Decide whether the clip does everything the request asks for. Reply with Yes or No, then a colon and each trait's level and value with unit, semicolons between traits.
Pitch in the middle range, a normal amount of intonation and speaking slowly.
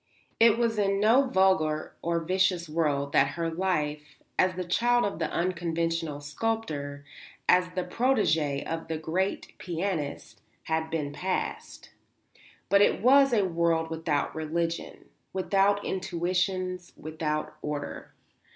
Yes: medium, 170 Hz; average, 3.4 semitones; slow, 125 wpm